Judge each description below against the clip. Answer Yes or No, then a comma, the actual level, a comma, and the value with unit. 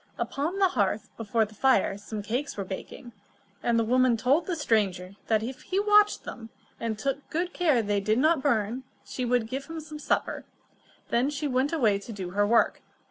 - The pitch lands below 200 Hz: No, high, 240 Hz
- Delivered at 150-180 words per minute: No, average, 195 wpm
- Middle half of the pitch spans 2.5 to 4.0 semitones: No, average, 5.3 semitones